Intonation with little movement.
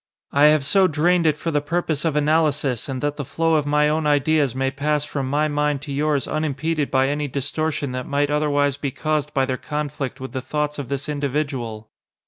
Yes: narrow, 1.6 semitones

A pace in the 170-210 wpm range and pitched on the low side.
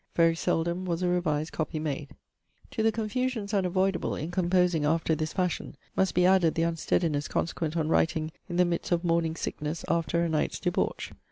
No: average, 180 wpm; medium, 170 Hz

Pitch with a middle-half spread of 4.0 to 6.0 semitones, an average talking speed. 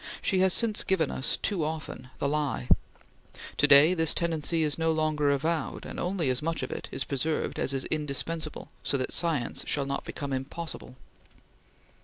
No: average, 2.9 semitones; average, 175 wpm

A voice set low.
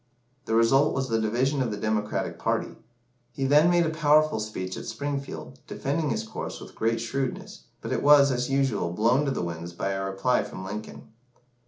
Yes: low, 125 Hz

